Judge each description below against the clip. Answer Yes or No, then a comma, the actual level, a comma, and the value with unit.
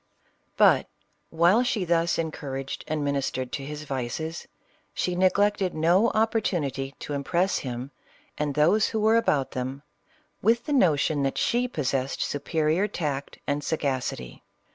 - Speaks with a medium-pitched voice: Yes, medium, 155 Hz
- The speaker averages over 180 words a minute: No, slow, 135 wpm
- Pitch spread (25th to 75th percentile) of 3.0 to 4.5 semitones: No, average, 5.3 semitones